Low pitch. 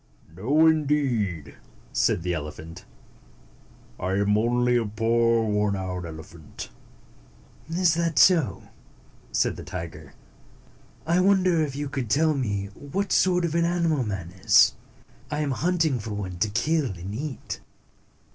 Yes: low, 120 Hz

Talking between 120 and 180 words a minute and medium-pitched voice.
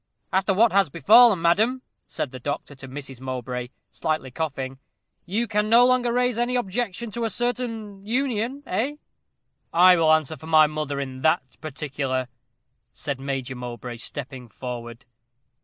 Yes: average, 150 wpm; medium, 160 Hz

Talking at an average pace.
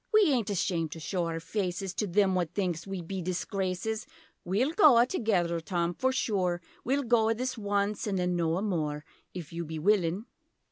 Yes: average, 180 wpm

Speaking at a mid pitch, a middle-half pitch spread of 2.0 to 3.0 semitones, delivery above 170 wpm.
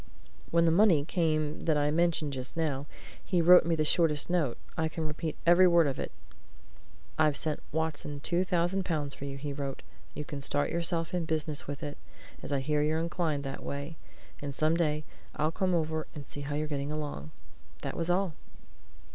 Yes: medium, 155 Hz; narrow, 2.6 semitones; average, 195 wpm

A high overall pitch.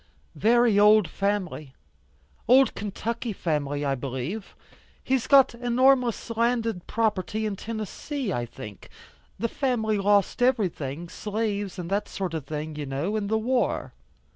Yes: high, 210 Hz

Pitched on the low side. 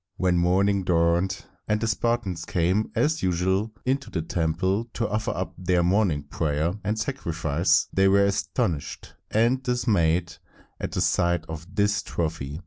Yes: very low, 90 Hz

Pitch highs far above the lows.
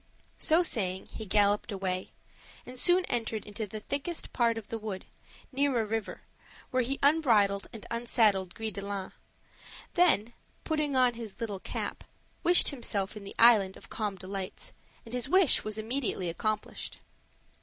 No: average, 4.1 semitones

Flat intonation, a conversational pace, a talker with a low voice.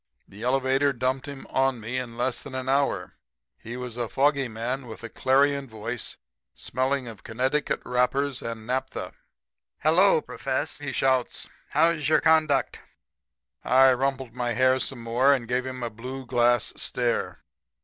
Yes: narrow, 2.1 semitones; average, 155 wpm; low, 130 Hz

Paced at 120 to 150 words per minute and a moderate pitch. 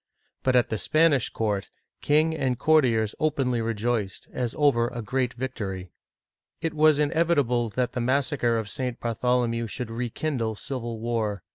No: average, 145 wpm; low, 125 Hz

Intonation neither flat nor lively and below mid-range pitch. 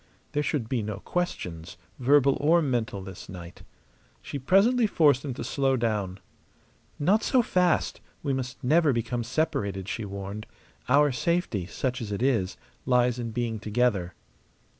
No: wide, 5.7 semitones; low, 125 Hz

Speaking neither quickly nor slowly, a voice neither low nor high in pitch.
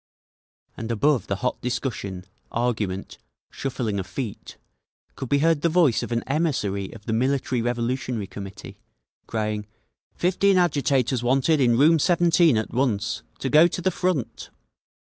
No: average, 145 wpm; low, 125 Hz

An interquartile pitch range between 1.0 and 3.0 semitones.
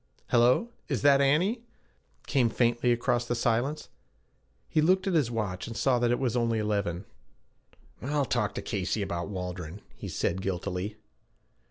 No: average, 5.1 semitones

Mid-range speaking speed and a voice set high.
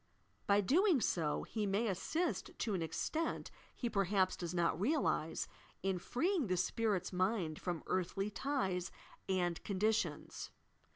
No: slow, 130 wpm; high, 195 Hz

